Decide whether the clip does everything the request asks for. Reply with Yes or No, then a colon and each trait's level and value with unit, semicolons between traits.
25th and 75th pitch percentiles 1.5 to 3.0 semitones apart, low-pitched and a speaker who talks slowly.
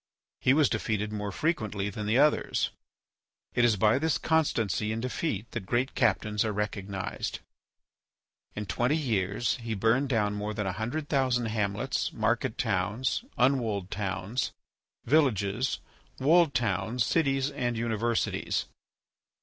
No: average, 4.1 semitones; low, 115 Hz; slow, 130 wpm